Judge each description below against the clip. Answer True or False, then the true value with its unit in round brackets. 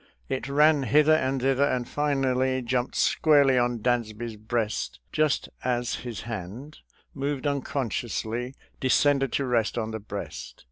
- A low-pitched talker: True (130 Hz)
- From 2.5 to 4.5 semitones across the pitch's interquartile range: True (3.0 semitones)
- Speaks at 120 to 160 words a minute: True (140 wpm)